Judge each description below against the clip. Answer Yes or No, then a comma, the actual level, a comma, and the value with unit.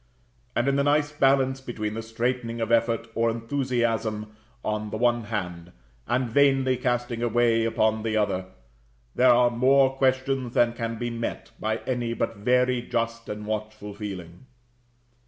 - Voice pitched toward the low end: Yes, low, 115 Hz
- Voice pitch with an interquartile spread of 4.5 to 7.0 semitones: No, narrow, 2.5 semitones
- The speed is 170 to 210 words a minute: No, average, 155 wpm